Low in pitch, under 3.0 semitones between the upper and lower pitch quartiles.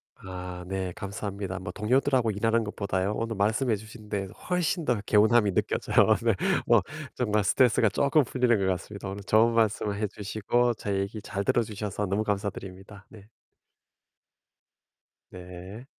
Yes: low, 105 Hz; narrow, 2.6 semitones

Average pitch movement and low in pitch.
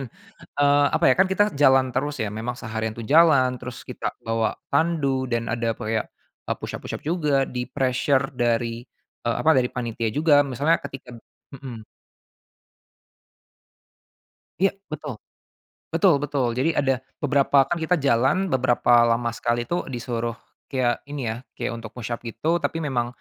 Yes: average, 3.7 semitones; low, 130 Hz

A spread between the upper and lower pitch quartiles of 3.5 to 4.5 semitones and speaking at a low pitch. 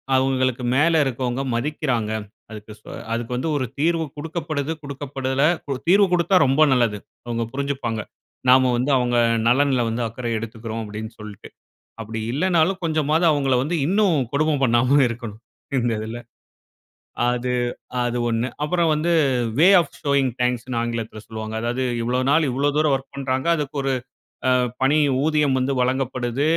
Yes: average, 3.8 semitones; low, 130 Hz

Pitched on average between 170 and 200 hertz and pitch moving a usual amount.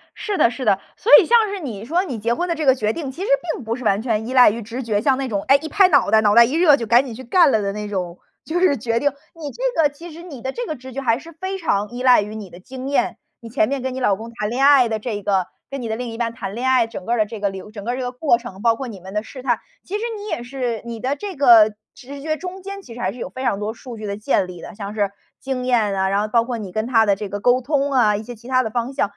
No: high, 240 Hz; average, 4.4 semitones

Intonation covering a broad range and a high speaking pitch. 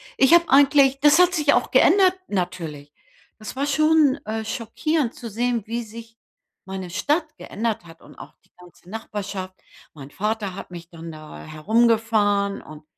Yes: wide, 6.7 semitones; high, 220 Hz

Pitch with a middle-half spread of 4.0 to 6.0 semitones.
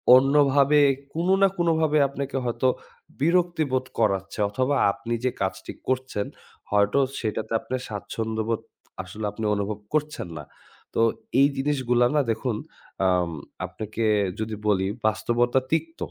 Yes: average, 5.0 semitones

